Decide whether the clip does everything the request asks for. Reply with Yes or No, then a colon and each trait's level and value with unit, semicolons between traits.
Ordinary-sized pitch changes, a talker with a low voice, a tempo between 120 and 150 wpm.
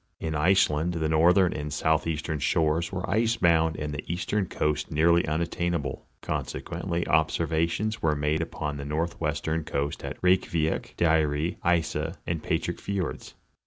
No: narrow, 2.1 semitones; very low, 80 Hz; average, 140 wpm